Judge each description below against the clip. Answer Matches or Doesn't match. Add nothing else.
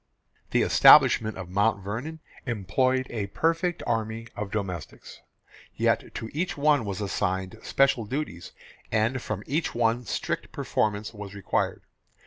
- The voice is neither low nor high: Doesn't match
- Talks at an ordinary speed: Doesn't match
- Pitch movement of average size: Matches